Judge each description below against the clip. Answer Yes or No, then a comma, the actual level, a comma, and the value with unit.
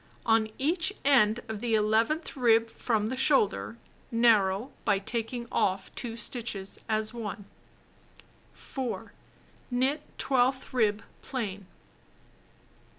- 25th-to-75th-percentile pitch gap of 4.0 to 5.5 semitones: No, average, 3.3 semitones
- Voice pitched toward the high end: Yes, high, 230 Hz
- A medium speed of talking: No, slow, 105 wpm